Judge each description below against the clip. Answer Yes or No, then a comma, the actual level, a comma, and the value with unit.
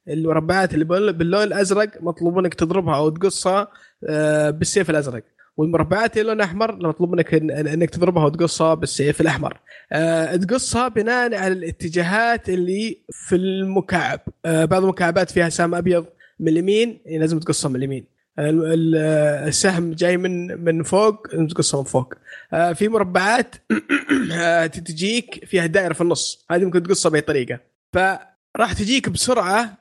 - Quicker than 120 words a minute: Yes, average, 130 wpm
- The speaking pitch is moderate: Yes, medium, 175 Hz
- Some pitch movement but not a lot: Yes, average, 3.6 semitones